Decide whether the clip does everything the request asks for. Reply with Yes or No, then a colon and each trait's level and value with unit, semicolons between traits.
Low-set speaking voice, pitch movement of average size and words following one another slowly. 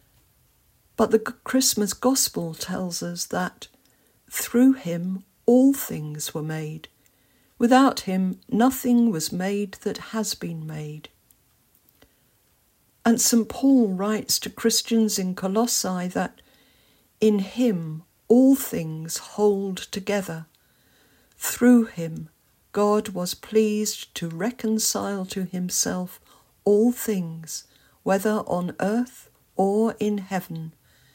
No: high, 205 Hz; average, 4.2 semitones; slow, 105 wpm